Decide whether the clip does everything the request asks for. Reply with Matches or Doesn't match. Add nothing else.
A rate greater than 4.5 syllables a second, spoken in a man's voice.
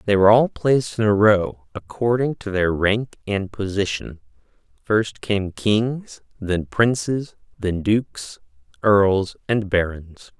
Doesn't match